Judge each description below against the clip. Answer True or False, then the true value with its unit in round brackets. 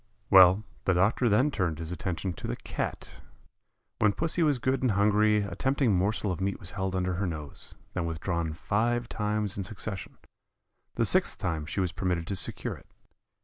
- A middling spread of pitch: True (3.2 semitones)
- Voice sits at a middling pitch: False (95 Hz)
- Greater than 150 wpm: True (185 wpm)